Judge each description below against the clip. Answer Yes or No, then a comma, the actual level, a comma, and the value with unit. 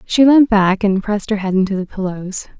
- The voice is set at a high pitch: Yes, high, 205 Hz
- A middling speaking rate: No, fast, 230 wpm